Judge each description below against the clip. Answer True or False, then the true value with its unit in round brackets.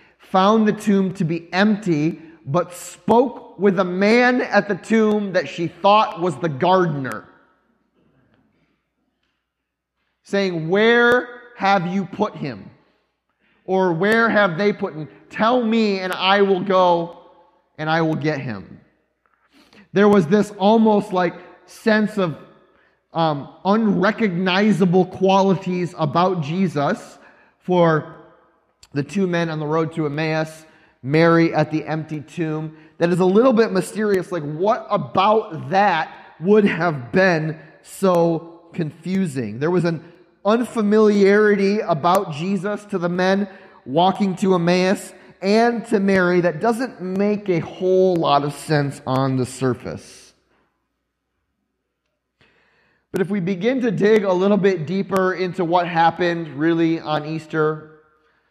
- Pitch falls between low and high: True (180 Hz)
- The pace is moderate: False (130 wpm)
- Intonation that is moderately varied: True (3.9 semitones)